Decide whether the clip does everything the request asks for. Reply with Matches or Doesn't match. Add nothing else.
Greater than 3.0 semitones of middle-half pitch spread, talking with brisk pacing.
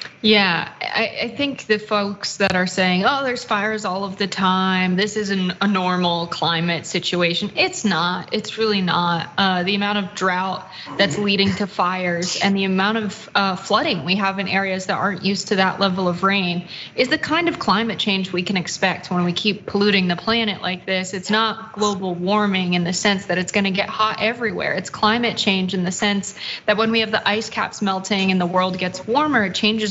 Doesn't match